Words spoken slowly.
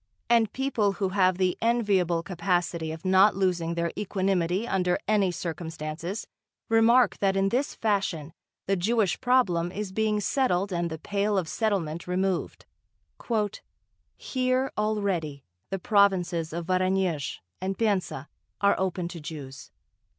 Yes: slow, 130 wpm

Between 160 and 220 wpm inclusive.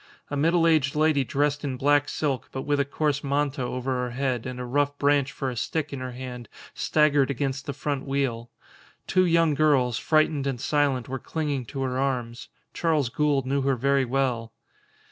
Yes: average, 190 wpm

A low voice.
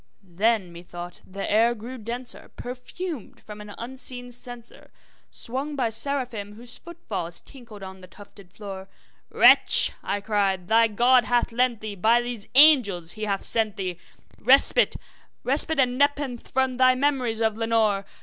No: high, 230 Hz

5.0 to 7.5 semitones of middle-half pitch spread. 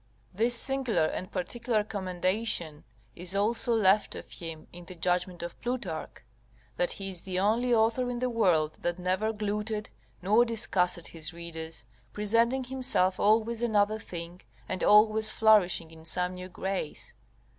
No: average, 4.0 semitones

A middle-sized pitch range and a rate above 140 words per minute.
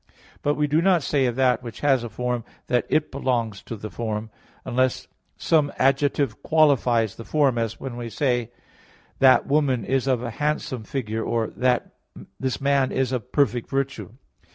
Yes: average, 3.2 semitones; average, 170 wpm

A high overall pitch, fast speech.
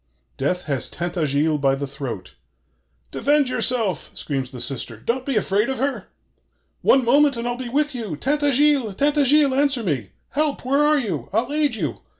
No: high, 240 Hz; average, 165 wpm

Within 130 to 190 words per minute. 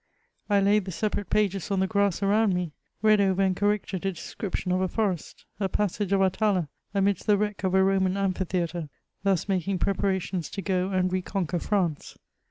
No: average, 200 wpm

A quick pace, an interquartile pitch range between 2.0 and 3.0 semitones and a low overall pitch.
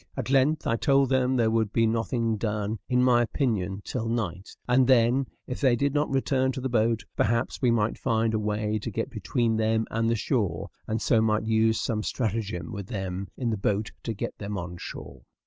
Yes: fast, 210 wpm; average, 2.7 semitones; low, 115 Hz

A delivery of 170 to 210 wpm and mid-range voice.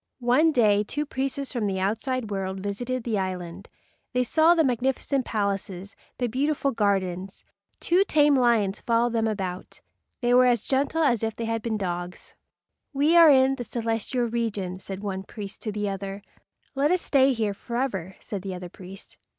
No: average, 175 wpm; high, 225 Hz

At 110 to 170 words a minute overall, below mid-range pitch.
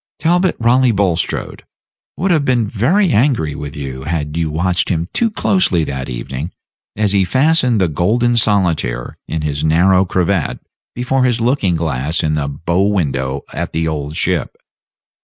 Yes: average, 155 wpm; very low, 90 Hz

